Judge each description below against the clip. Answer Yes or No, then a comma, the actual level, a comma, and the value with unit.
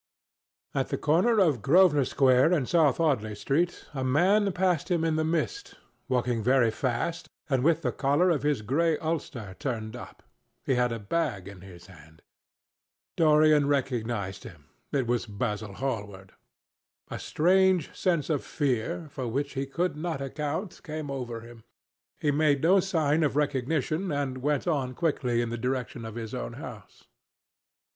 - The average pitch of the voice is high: No, medium, 140 Hz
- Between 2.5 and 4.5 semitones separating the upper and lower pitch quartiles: No, average, 5.2 semitones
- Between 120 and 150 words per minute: No, average, 160 wpm